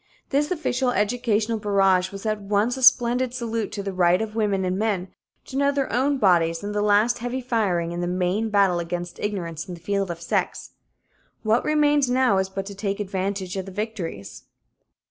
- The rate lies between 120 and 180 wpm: No, average, 195 wpm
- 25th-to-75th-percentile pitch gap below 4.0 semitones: No, average, 4.3 semitones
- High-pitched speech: Yes, high, 205 Hz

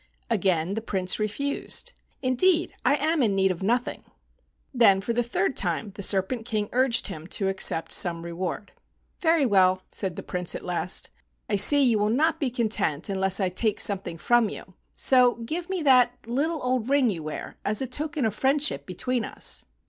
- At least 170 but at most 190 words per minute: Yes, average, 185 wpm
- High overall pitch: Yes, high, 220 Hz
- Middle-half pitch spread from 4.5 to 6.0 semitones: Yes, average, 5.3 semitones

